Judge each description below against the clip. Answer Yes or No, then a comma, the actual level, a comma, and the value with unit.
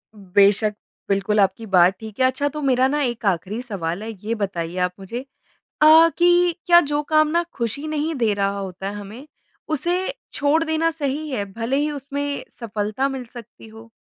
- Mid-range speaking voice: No, high, 240 Hz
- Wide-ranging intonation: Yes, wide, 6.5 semitones